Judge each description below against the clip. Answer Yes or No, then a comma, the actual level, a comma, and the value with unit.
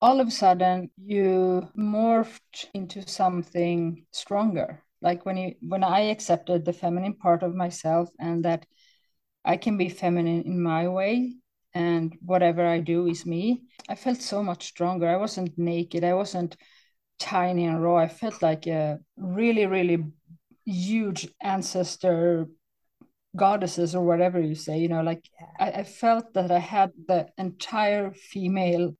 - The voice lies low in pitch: No, medium, 180 Hz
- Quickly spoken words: No, average, 150 wpm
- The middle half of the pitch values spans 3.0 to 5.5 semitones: No, narrow, 2.4 semitones